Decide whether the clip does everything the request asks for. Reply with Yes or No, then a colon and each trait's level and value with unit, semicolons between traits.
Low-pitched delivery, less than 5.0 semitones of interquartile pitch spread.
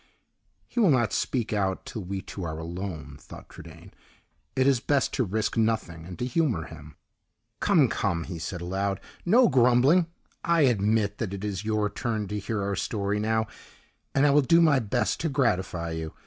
No: low, 105 Hz; wide, 5.4 semitones